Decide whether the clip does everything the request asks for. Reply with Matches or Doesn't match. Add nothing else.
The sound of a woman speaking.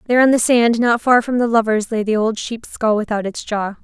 Matches